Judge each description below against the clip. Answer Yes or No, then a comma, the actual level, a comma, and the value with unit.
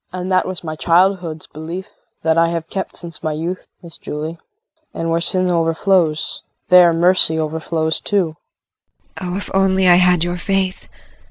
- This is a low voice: No, medium, 175 Hz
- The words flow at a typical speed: Yes, average, 165 wpm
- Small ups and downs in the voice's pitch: Yes, narrow, 2.2 semitones